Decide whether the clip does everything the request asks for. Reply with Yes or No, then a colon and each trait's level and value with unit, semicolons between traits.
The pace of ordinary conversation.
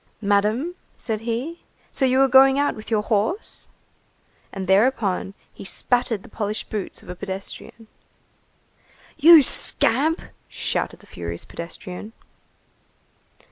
No: slow, 120 wpm